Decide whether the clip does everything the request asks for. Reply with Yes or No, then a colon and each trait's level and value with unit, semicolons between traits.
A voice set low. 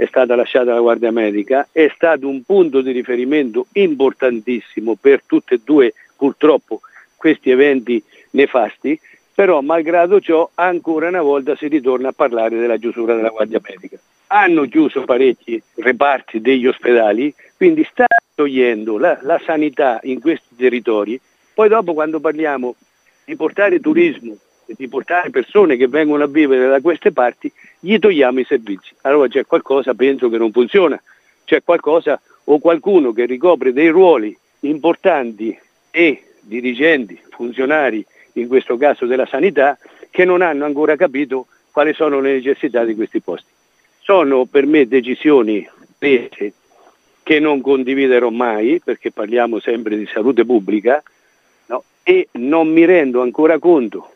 No: medium, 155 Hz